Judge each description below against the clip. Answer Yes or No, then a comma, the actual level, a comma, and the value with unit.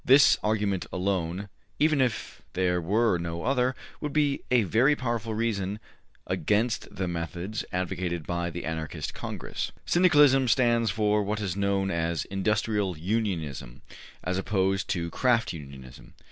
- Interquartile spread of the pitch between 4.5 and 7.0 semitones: Yes, average, 4.9 semitones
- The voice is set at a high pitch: No, low, 100 Hz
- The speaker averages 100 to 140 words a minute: Yes, slow, 135 wpm